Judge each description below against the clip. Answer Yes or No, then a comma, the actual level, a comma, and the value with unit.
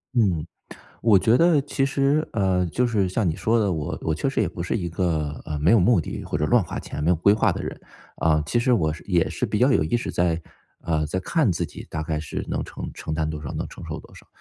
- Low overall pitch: Yes, very low, 90 Hz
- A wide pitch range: Yes, wide, 6.5 semitones